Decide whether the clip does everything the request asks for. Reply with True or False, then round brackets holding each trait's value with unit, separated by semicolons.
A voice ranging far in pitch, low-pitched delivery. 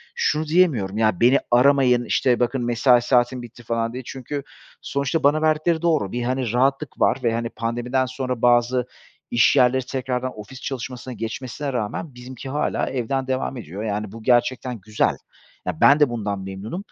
False (2.4 semitones; 125 Hz)